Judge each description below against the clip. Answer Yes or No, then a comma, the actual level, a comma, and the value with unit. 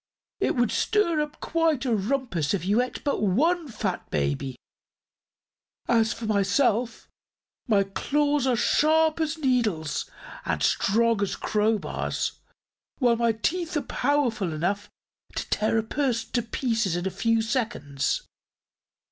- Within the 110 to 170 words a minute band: Yes, slow, 135 wpm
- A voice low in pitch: No, high, 230 Hz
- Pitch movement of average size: No, wide, 5.7 semitones